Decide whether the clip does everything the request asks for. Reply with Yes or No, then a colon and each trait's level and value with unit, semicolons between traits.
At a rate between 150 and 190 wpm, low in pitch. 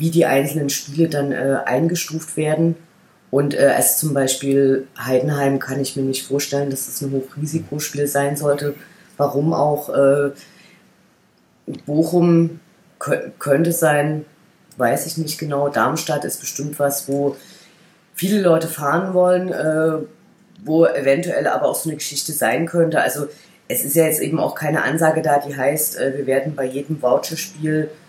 No: average, 155 wpm; medium, 150 Hz